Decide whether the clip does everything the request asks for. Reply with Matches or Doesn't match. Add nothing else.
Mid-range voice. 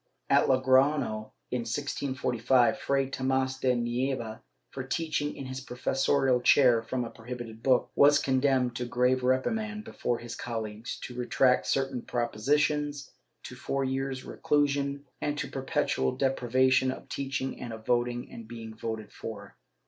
Doesn't match